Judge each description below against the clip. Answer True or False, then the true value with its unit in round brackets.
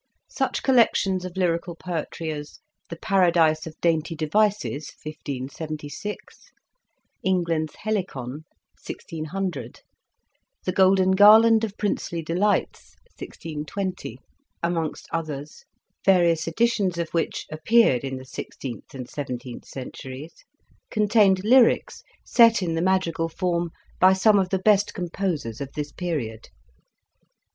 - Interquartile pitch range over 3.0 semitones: True (4.0 semitones)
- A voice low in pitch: False (170 Hz)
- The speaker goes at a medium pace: False (115 wpm)